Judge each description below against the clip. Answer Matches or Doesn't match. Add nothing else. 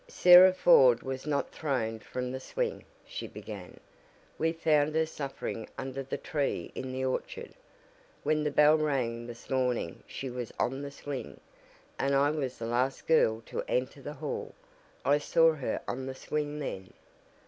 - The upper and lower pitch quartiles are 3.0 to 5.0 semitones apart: Matches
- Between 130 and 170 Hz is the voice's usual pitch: Matches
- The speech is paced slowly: Doesn't match